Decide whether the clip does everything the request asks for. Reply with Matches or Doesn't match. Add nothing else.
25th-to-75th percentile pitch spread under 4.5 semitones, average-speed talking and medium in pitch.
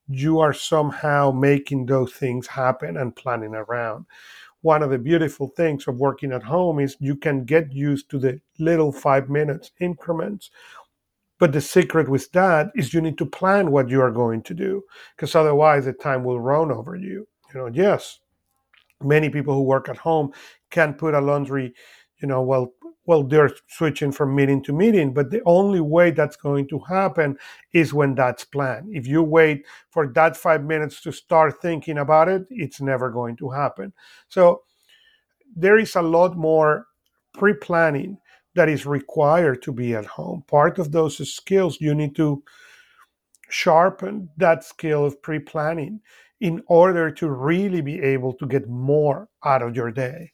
Matches